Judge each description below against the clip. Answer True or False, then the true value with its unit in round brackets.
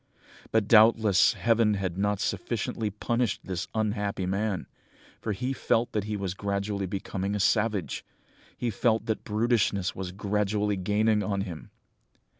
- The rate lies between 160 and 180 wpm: False (140 wpm)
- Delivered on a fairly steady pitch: True (2.0 semitones)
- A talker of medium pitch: False (105 Hz)